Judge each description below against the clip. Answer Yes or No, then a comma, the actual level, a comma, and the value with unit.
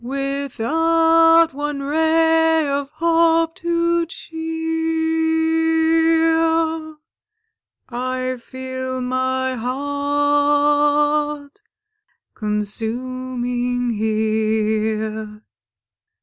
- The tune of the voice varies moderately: Yes, average, 4.2 semitones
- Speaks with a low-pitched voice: No, very high, 290 Hz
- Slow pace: Yes, slow, 50 wpm